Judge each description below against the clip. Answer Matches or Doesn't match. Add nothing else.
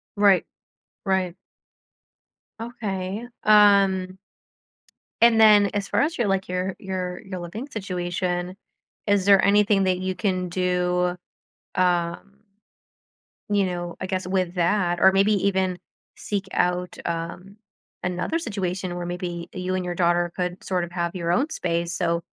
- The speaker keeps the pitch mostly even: Matches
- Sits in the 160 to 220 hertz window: Matches